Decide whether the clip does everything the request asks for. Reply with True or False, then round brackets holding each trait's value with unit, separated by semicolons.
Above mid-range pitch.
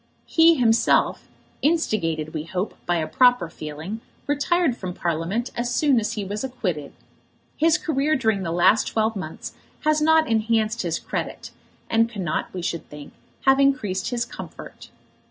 True (220 Hz)